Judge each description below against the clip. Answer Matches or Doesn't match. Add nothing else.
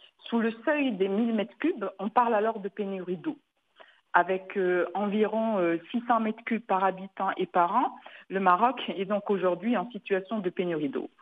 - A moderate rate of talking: Matches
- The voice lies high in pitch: Matches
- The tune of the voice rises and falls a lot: Doesn't match